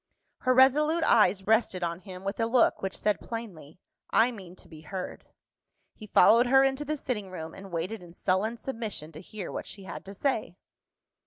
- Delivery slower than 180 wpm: No, average, 190 wpm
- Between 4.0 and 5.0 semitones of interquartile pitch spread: Yes, average, 4.7 semitones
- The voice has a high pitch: Yes, high, 210 Hz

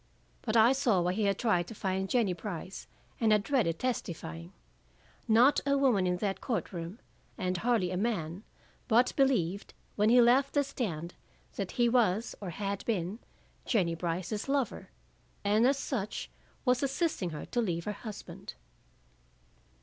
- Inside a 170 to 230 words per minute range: No, average, 155 wpm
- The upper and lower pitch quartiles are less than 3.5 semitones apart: No, average, 5.1 semitones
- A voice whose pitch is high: Yes, high, 210 Hz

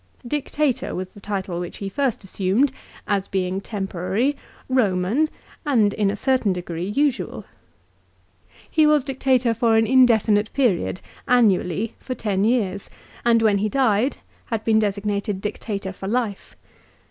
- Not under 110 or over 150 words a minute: Yes, average, 140 wpm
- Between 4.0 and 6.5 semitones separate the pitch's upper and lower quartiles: Yes, average, 4.4 semitones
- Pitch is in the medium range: No, high, 215 Hz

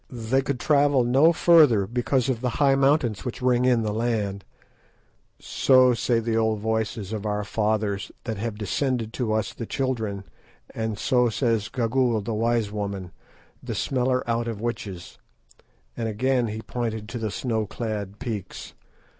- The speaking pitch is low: Yes, low, 115 Hz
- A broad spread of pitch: No, average, 2.9 semitones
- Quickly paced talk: No, average, 160 wpm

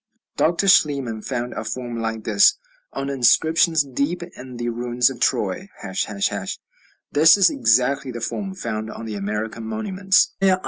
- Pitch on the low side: Yes, low, 125 Hz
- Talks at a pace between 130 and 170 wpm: Yes, average, 145 wpm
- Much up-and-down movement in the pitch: Yes, wide, 6.1 semitones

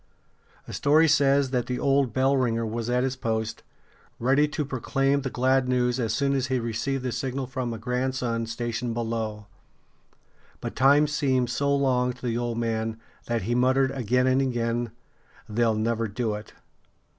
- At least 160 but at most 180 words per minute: Yes, average, 170 wpm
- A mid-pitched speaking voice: No, low, 125 Hz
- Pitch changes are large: No, narrow, 2.5 semitones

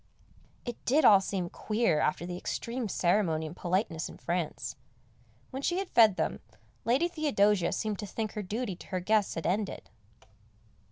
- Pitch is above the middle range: Yes, high, 205 Hz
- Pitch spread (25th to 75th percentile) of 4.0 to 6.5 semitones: Yes, average, 4.7 semitones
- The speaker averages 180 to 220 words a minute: No, average, 165 wpm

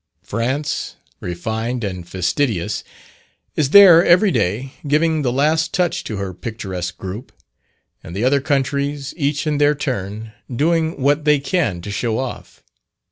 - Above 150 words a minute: No, average, 140 wpm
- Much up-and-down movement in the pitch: Yes, wide, 6.4 semitones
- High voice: No, low, 130 Hz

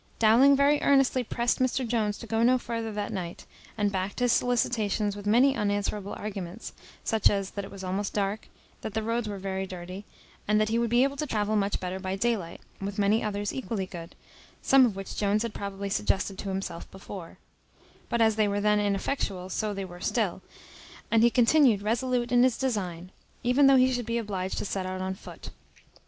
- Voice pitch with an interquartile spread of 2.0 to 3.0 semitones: No, average, 3.4 semitones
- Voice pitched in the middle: No, high, 210 Hz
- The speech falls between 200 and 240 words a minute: Yes, fast, 205 wpm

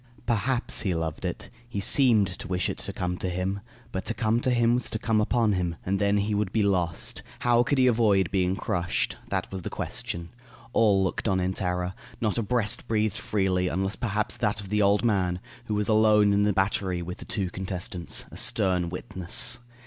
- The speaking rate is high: Yes, fast, 210 wpm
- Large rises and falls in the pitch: No, average, 3.0 semitones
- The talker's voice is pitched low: Yes, low, 100 Hz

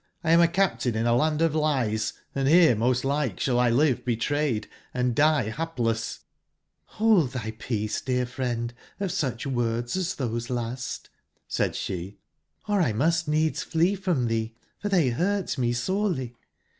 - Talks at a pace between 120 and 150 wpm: Yes, average, 145 wpm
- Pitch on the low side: Yes, low, 130 Hz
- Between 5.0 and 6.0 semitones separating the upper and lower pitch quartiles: Yes, wide, 5.6 semitones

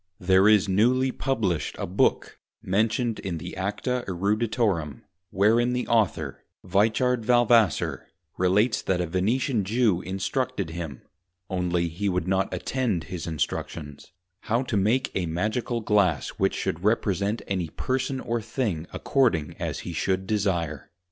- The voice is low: Yes, low, 100 Hz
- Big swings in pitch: No, average, 4.7 semitones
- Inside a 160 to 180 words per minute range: No, slow, 135 wpm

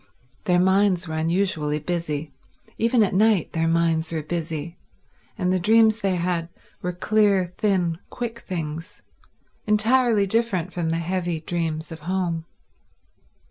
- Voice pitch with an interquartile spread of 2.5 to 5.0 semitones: Yes, average, 3.5 semitones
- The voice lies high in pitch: No, medium, 180 Hz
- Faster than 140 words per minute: No, slow, 135 wpm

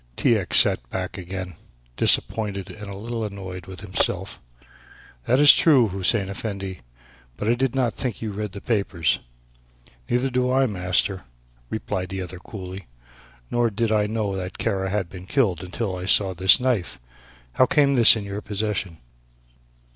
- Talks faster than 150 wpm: Yes, average, 160 wpm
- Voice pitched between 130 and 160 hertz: No, low, 100 Hz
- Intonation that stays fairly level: No, average, 3.6 semitones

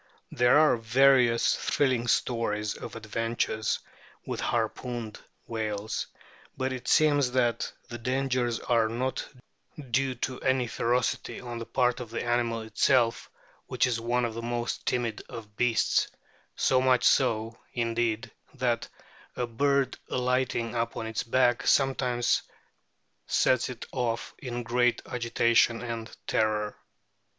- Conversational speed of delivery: No, slow, 125 wpm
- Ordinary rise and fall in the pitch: No, narrow, 1.8 semitones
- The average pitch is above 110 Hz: Yes, low, 120 Hz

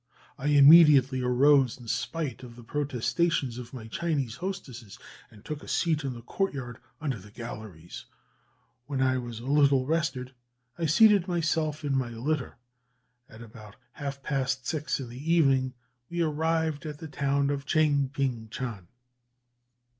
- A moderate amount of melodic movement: Yes, average, 3.9 semitones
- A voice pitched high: No, low, 135 Hz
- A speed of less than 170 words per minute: Yes, average, 155 wpm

